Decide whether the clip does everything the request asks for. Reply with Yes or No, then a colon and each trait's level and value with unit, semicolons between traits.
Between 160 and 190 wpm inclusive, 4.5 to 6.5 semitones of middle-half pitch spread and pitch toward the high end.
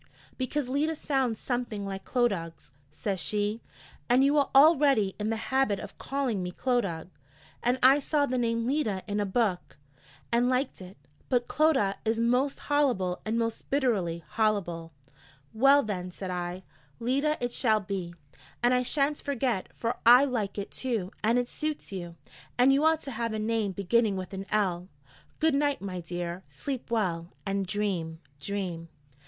Yes: average, 165 wpm; wide, 5.4 semitones; high, 225 Hz